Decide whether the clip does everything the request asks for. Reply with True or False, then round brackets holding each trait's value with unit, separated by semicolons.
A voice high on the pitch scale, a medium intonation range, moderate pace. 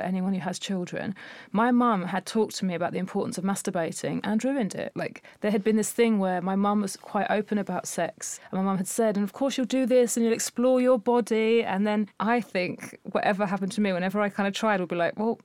False (210 Hz; 3.6 semitones; 255 wpm)